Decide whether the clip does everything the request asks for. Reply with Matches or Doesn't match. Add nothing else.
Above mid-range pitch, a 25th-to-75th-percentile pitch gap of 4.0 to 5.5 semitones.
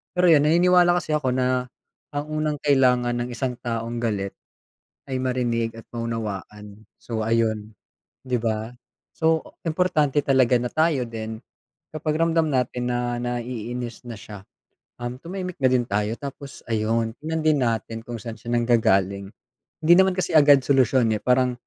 Doesn't match